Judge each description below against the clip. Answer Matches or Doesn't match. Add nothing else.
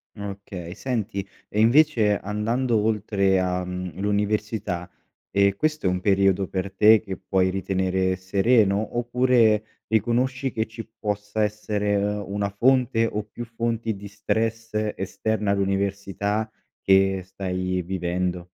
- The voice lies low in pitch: Matches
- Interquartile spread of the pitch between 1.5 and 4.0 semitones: Matches